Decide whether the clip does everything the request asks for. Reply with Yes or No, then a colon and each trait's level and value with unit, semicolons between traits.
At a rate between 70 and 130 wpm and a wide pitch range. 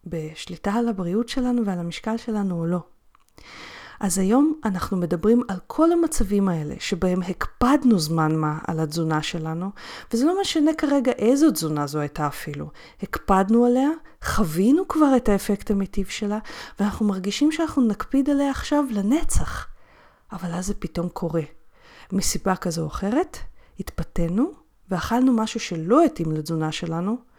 No: average, 140 wpm; wide, 6.2 semitones